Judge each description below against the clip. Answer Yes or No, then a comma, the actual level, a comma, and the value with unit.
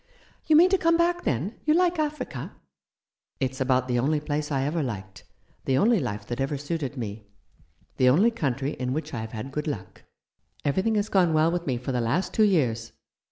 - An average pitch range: No, wide, 7.6 semitones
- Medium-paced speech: No, fast, 220 wpm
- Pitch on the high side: No, medium, 145 Hz